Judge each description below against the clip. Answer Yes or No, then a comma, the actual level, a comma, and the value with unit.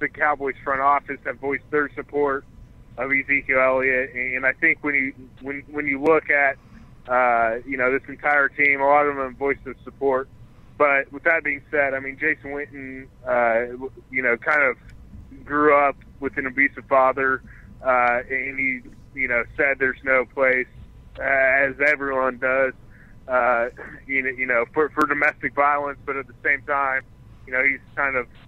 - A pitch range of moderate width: No, narrow, 2.2 semitones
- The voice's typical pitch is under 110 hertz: No, low, 135 Hz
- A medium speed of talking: Yes, average, 180 wpm